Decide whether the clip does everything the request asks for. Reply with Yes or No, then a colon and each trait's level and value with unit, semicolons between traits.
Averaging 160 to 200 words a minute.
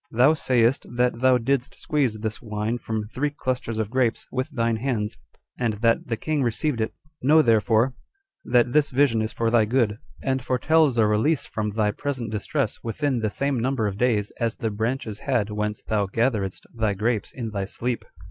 Yes: average, 185 wpm